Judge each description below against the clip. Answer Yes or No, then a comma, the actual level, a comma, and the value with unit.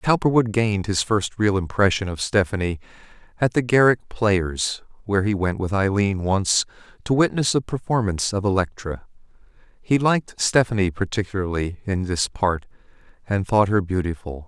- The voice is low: Yes, low, 100 Hz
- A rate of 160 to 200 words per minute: No, average, 145 wpm